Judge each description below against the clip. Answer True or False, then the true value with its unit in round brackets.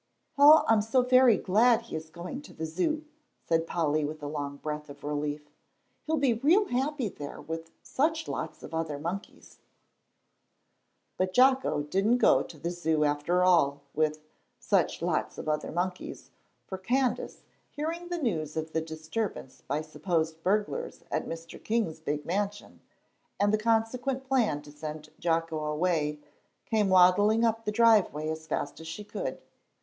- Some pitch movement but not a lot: False (6.9 semitones)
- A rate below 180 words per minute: True (160 wpm)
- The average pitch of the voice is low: False (180 Hz)